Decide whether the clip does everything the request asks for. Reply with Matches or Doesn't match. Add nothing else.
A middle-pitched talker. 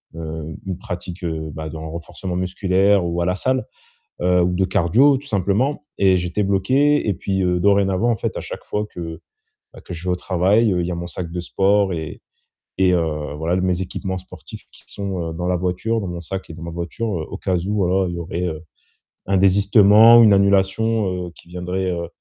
Doesn't match